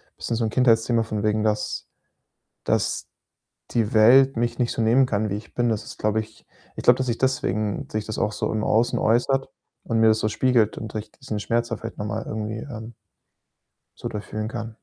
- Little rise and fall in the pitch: Yes, narrow, 1.7 semitones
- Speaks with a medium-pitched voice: No, low, 110 Hz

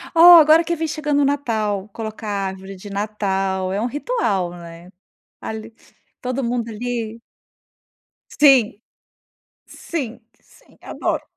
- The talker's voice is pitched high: Yes, high, 225 Hz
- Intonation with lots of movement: Yes, wide, 6.3 semitones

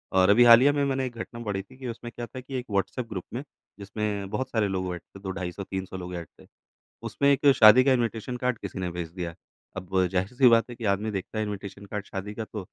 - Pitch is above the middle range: No, low, 105 Hz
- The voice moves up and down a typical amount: Yes, average, 4.2 semitones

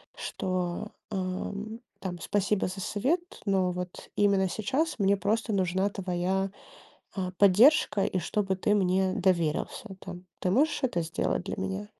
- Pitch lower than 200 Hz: Yes, high, 190 Hz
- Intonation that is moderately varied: No, narrow, 2.2 semitones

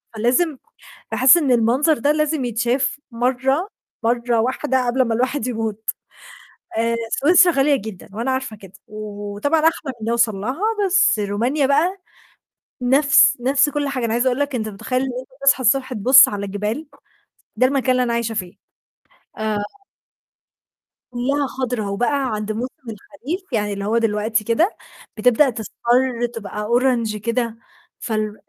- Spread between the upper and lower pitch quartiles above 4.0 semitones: No, average, 3.7 semitones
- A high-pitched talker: Yes, high, 245 Hz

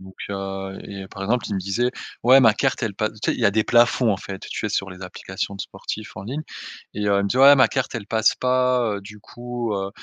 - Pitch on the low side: Yes, low, 105 Hz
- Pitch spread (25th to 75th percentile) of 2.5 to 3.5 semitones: No, average, 3.9 semitones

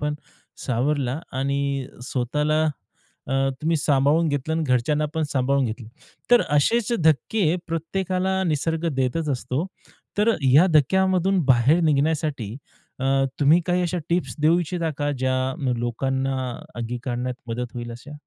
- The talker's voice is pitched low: No, medium, 145 Hz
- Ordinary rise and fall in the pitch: Yes, average, 4.1 semitones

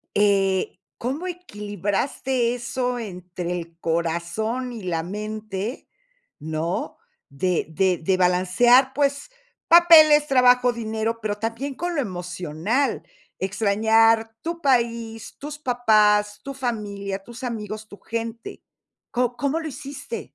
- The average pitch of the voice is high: Yes, high, 225 Hz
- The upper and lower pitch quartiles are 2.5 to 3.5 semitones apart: No, average, 4.8 semitones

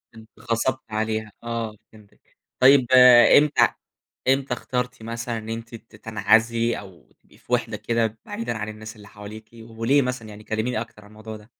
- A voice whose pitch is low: Yes, low, 115 Hz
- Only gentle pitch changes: Yes, narrow, 1.5 semitones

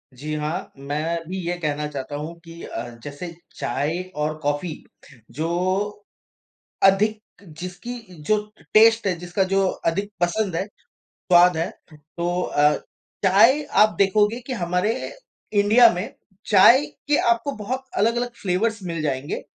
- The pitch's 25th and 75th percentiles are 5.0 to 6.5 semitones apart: Yes, wide, 5.6 semitones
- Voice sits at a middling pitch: Yes, medium, 180 Hz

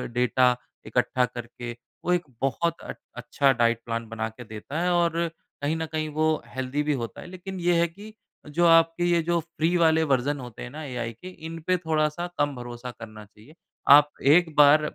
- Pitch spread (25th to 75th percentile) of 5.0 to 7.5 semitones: Yes, average, 5.3 semitones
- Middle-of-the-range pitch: Yes, medium, 145 Hz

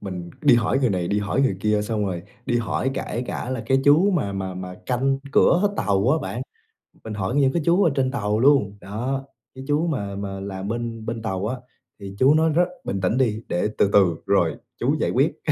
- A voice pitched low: Yes, low, 115 Hz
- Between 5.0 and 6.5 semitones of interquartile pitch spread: Yes, average, 5.3 semitones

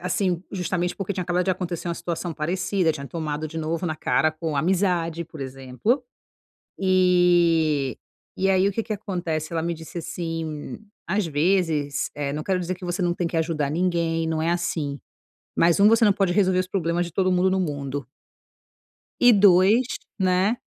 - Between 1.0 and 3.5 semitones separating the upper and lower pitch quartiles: Yes, average, 2.8 semitones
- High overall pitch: No, medium, 175 Hz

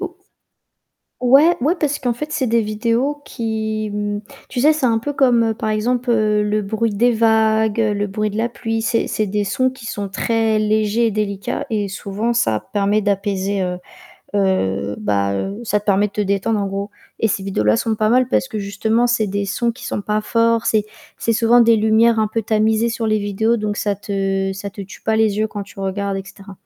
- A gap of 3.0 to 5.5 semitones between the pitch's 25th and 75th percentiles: No, narrow, 2.4 semitones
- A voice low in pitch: No, high, 215 Hz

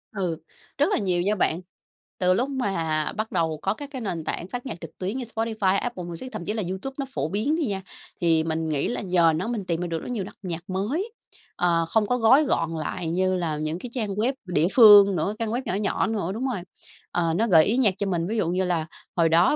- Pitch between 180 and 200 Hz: Yes, high, 190 Hz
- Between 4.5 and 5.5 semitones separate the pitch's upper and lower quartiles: Yes, average, 5.0 semitones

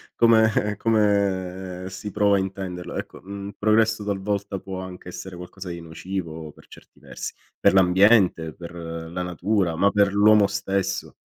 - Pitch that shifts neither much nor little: No, narrow, 2.3 semitones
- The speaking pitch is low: Yes, very low, 95 Hz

